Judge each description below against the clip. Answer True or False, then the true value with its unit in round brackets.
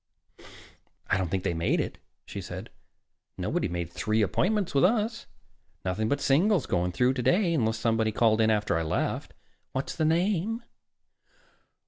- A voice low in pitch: True (115 Hz)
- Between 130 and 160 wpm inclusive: True (150 wpm)